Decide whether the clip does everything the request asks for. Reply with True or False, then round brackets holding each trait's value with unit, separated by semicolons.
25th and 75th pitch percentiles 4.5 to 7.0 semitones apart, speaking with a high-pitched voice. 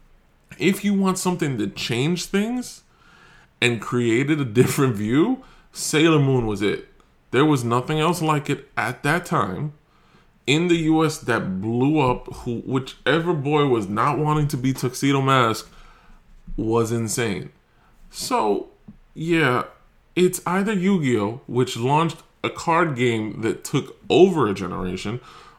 False (5.2 semitones; 140 Hz)